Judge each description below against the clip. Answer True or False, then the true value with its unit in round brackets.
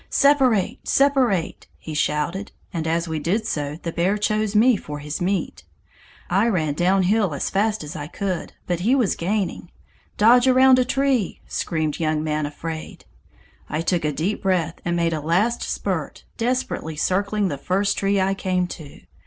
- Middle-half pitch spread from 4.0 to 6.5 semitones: True (5.1 semitones)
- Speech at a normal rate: True (170 wpm)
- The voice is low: False (185 Hz)